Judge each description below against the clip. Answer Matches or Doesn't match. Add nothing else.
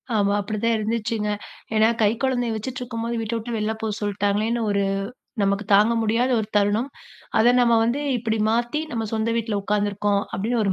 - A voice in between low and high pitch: Doesn't match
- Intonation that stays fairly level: Matches